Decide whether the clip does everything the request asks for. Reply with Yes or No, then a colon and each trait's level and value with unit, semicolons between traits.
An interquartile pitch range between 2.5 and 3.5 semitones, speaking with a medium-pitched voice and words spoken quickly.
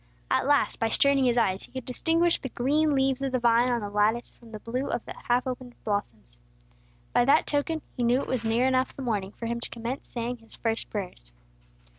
No: average, 2.8 semitones; high, 245 Hz; fast, 225 wpm